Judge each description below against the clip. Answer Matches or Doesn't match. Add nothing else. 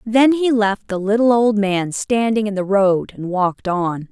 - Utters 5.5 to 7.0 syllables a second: Doesn't match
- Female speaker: Matches